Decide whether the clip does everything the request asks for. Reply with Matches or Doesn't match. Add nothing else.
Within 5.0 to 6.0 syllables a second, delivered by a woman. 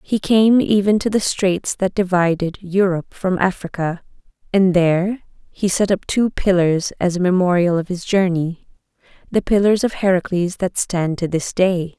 Doesn't match